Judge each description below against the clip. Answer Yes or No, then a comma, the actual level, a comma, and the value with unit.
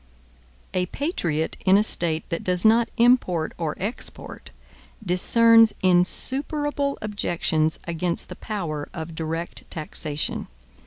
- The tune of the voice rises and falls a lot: Yes, wide, 5.8 semitones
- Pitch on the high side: No, medium, 180 Hz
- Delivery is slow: Yes, slow, 110 wpm